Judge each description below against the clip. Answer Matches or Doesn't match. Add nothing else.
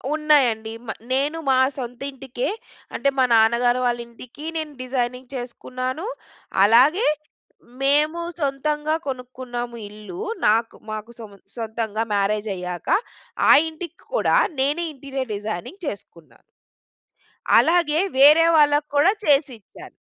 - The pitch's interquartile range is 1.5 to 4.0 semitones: Doesn't match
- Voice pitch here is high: Matches